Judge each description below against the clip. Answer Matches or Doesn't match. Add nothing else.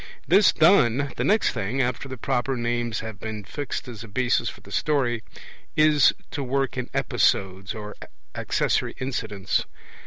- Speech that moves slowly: Doesn't match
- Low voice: Matches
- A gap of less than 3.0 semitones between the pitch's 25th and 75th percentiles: Doesn't match